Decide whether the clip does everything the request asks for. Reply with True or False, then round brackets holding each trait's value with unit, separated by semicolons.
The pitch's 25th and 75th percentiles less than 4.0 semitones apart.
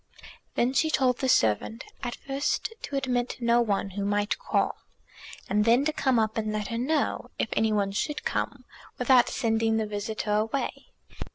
True (3.6 semitones)